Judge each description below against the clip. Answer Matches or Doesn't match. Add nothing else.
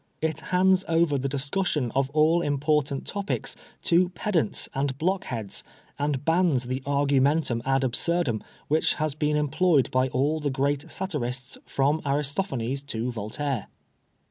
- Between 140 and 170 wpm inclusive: Matches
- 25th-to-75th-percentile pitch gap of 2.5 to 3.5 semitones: Matches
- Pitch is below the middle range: Doesn't match